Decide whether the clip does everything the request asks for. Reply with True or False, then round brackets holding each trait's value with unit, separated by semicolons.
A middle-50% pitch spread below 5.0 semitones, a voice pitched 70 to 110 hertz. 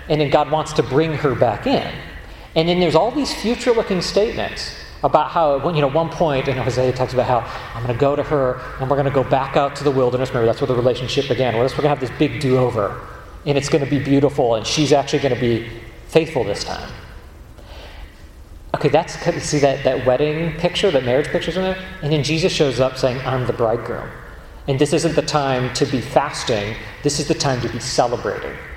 False (3.7 semitones; 140 Hz)